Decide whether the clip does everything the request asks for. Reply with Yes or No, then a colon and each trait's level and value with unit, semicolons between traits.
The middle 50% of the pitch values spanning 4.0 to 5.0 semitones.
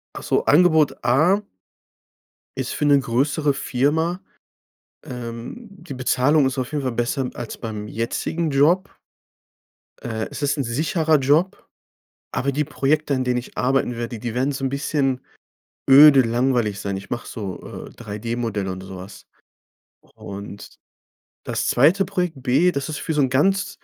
Yes: average, 4.4 semitones